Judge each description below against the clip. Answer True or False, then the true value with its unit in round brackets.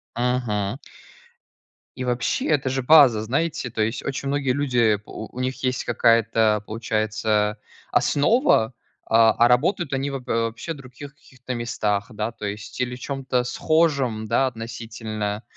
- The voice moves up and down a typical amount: True (3.4 semitones)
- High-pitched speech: False (120 Hz)